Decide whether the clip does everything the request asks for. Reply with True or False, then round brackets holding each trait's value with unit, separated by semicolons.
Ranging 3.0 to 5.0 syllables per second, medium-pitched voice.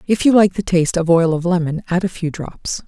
False (5.7 syllables/s; 175 Hz)